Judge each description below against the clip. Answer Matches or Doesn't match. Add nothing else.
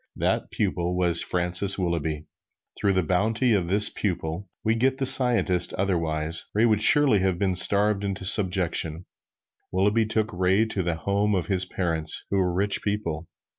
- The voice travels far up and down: Doesn't match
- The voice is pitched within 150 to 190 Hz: Doesn't match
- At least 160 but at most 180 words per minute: Matches